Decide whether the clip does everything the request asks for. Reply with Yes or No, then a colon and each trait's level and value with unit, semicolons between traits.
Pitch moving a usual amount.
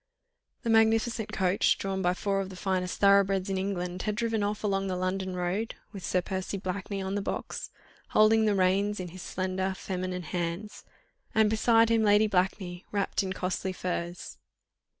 No: narrow, 2.1 semitones